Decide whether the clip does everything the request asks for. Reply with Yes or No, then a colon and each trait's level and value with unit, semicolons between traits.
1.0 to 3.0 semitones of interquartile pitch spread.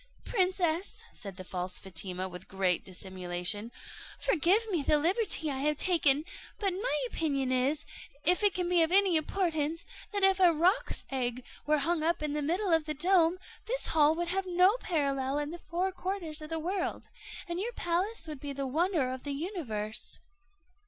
No: average, 5.1 semitones